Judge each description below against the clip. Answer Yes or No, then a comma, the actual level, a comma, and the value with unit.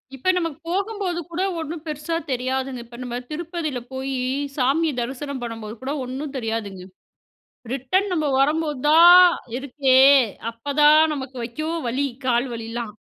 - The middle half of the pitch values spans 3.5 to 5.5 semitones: Yes, average, 4.4 semitones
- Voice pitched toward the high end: Yes, very high, 275 Hz